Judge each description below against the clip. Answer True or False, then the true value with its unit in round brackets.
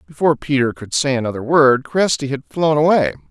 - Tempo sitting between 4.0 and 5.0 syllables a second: False (5.7 syllables/s)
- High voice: False (135 Hz)